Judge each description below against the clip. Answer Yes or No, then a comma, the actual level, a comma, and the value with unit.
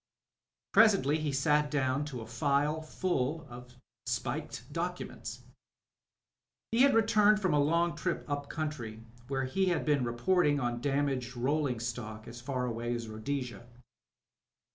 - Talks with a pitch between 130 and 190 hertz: Yes, medium, 140 Hz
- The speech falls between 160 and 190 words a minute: No, average, 140 wpm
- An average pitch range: Yes, average, 4.3 semitones